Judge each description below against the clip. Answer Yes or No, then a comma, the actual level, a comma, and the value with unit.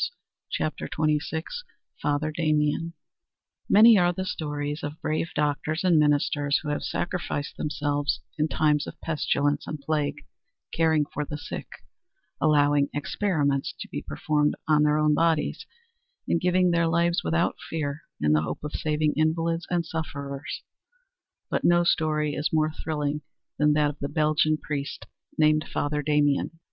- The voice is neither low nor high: Yes, medium, 150 Hz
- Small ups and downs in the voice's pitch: Yes, narrow, 1.6 semitones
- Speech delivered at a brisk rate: No, average, 145 wpm